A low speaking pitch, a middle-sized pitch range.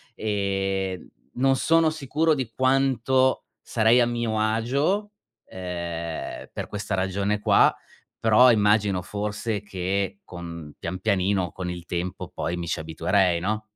Yes: low, 100 Hz; average, 4.5 semitones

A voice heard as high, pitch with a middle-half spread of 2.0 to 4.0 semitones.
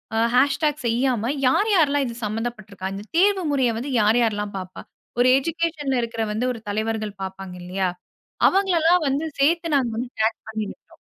No: high, 240 Hz; average, 5.3 semitones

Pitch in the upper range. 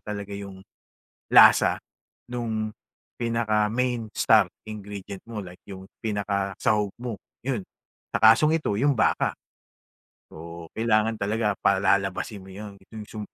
No: low, 105 Hz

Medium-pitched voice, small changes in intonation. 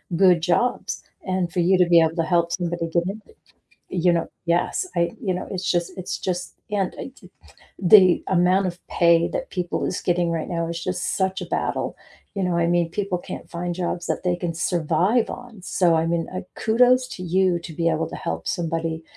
Yes: medium, 175 Hz; narrow, 1.8 semitones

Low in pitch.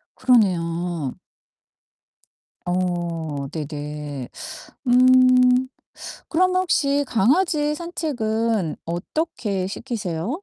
No: high, 215 Hz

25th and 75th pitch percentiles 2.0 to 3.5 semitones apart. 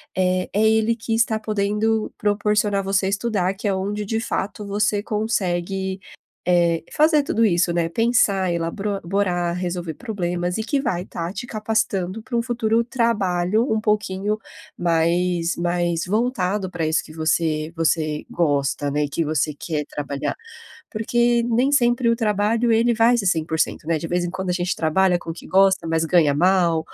No: average, 4.2 semitones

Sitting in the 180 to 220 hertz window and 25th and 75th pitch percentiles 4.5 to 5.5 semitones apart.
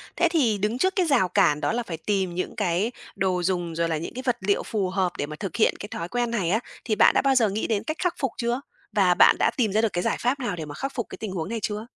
Yes: high, 210 Hz; average, 5.1 semitones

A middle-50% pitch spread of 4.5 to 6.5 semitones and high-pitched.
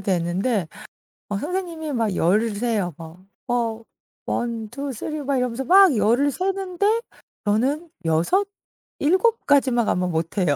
No: wide, 7.5 semitones; high, 240 Hz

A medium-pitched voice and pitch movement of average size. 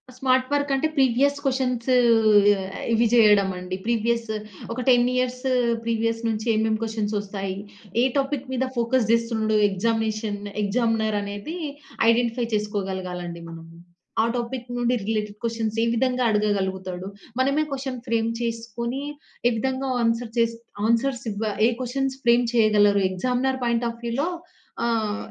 No: high, 230 Hz; average, 3.0 semitones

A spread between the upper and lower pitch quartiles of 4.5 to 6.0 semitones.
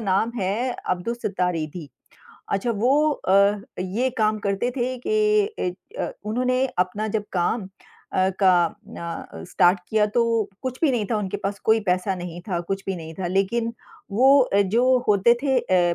Yes: average, 4.9 semitones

